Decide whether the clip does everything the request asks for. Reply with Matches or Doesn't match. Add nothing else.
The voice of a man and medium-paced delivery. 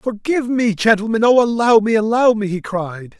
Matches